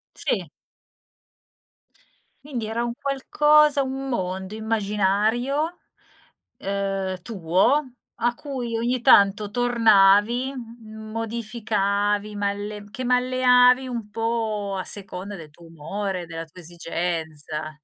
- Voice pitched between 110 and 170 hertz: No, high, 215 Hz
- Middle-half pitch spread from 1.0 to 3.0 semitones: No, average, 3.9 semitones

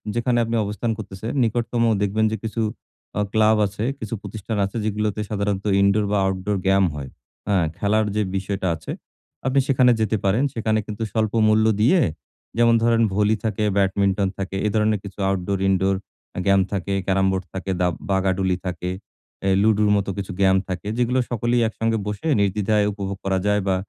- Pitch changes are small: Yes, narrow, 2.2 semitones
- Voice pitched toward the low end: Yes, low, 105 Hz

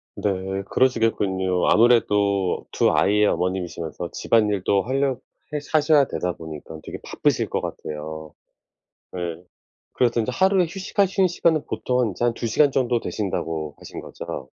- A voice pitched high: No, low, 105 Hz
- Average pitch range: No, wide, 6.6 semitones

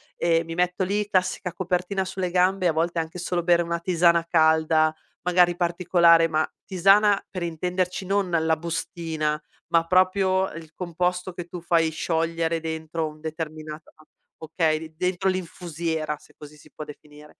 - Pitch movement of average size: No, narrow, 2.1 semitones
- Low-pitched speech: No, medium, 170 Hz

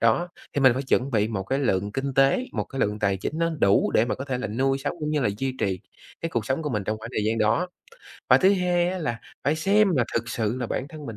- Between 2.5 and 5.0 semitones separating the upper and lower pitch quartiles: No, wide, 5.5 semitones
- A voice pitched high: No, low, 130 Hz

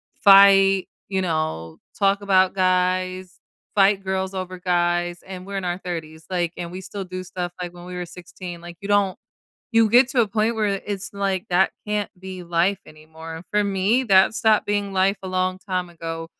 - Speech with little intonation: Yes, narrow, 2.1 semitones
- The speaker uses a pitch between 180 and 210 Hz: Yes, medium, 185 Hz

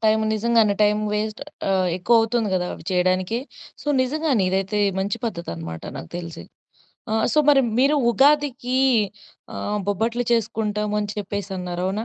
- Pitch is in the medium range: No, high, 210 Hz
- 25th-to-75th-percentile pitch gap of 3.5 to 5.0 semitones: Yes, average, 3.8 semitones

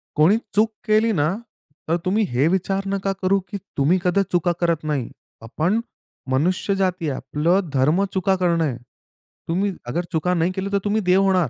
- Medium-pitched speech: Yes, medium, 180 Hz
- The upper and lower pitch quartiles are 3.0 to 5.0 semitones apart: Yes, average, 3.6 semitones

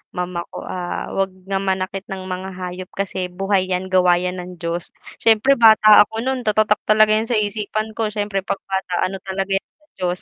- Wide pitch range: No, average, 2.7 semitones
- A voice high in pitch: Yes, high, 195 Hz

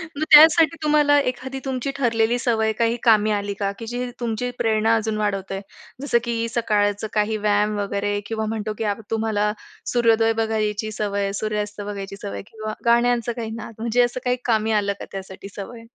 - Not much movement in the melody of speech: Yes, narrow, 2.3 semitones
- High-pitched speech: Yes, high, 220 Hz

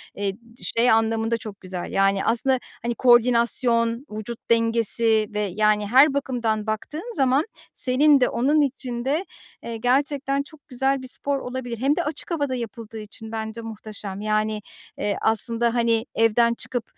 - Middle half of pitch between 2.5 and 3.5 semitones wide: Yes, average, 3.1 semitones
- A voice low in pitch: No, high, 235 Hz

